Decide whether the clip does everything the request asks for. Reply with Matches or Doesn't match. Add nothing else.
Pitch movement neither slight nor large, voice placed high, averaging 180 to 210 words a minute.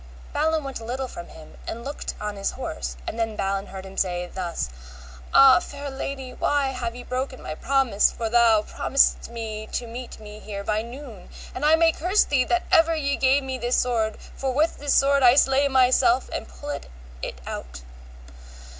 Matches